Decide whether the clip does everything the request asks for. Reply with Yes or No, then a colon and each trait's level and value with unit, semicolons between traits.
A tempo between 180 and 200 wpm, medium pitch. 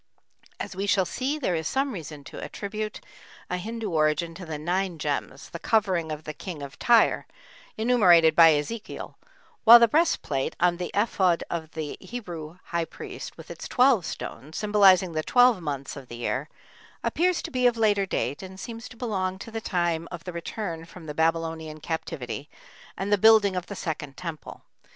Yes: average, 185 wpm; medium, 180 Hz